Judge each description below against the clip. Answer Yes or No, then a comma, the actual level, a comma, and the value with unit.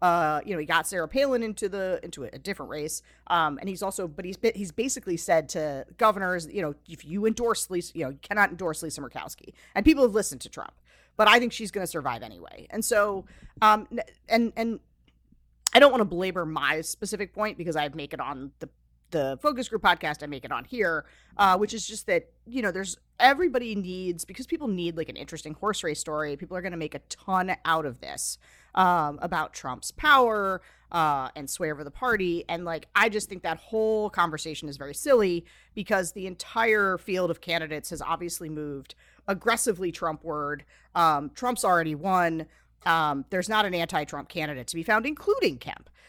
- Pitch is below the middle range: No, medium, 185 Hz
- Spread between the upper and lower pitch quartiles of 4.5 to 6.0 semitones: Yes, average, 5.3 semitones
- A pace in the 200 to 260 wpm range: Yes, fast, 205 wpm